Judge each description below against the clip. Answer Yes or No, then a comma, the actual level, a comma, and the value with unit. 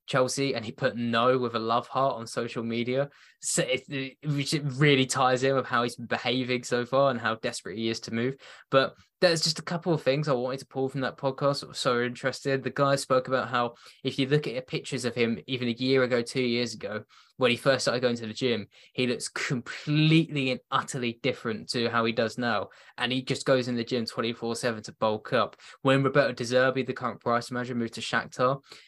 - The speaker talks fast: Yes, fast, 230 wpm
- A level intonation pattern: Yes, narrow, 2.2 semitones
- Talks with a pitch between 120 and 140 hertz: Yes, low, 130 Hz